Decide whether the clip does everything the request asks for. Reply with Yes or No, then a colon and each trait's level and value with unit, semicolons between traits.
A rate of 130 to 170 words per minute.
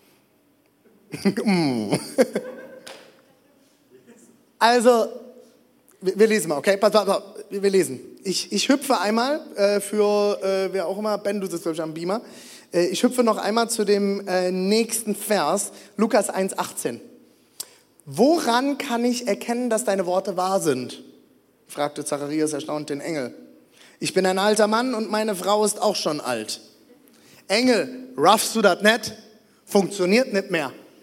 Yes: average, 145 wpm